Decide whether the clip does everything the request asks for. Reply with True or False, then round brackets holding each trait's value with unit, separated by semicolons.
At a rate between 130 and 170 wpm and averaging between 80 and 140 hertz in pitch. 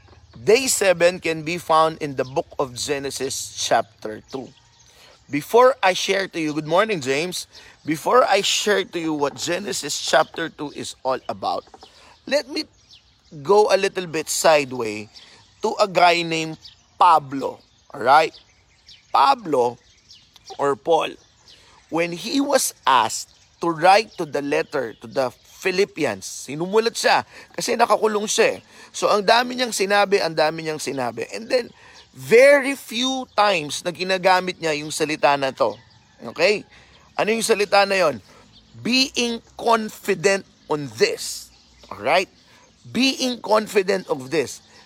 False (135 wpm; 185 Hz)